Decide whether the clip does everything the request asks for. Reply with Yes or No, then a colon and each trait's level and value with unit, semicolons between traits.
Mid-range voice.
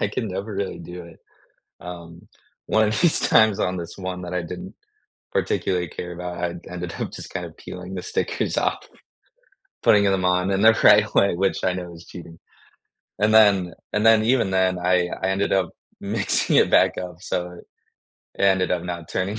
No: very low, 90 Hz